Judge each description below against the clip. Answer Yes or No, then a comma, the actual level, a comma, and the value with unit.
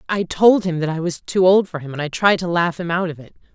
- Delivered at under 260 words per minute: No, fast, 320 wpm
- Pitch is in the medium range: Yes, medium, 175 Hz